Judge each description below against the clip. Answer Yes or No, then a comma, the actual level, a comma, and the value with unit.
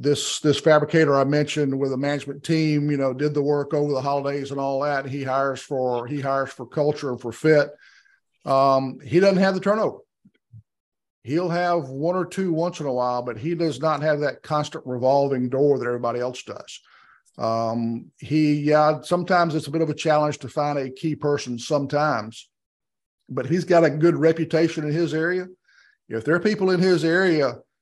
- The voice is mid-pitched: Yes, medium, 145 Hz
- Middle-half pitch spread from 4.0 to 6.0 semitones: No, average, 3.2 semitones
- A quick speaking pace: No, average, 195 wpm